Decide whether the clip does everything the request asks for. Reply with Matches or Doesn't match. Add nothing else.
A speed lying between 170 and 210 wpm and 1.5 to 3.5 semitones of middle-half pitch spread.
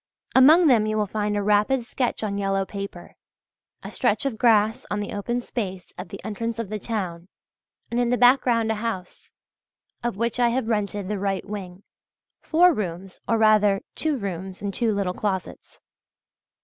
Matches